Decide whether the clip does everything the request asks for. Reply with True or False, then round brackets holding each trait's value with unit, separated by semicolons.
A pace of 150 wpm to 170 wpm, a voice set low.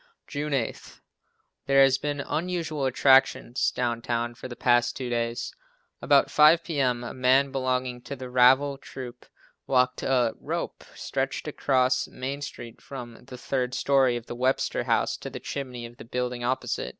True (160 wpm; 130 Hz)